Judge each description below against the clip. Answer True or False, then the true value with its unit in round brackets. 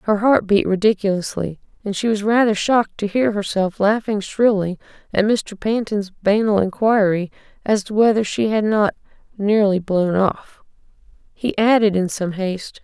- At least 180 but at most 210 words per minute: False (155 wpm)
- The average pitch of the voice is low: False (205 Hz)